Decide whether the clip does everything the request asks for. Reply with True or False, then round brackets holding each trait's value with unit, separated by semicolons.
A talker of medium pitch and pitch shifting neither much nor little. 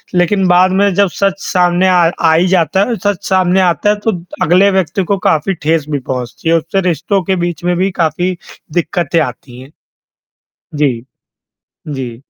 True (175 Hz; 3.1 semitones)